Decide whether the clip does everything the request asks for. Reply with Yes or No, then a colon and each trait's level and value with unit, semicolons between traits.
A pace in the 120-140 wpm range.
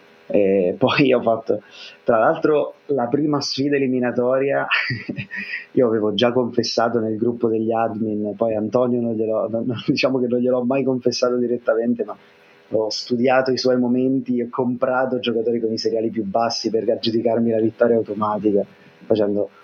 No: average, 155 wpm